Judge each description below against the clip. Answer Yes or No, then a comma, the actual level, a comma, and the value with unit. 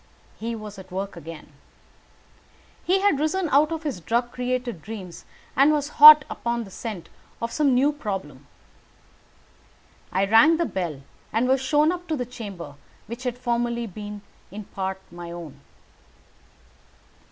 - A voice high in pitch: Yes, high, 235 Hz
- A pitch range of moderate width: No, wide, 6.7 semitones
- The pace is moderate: Yes, average, 150 wpm